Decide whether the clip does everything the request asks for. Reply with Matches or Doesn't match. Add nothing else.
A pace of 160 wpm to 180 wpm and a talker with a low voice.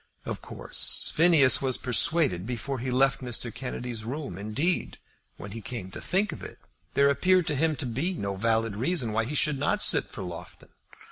Doesn't match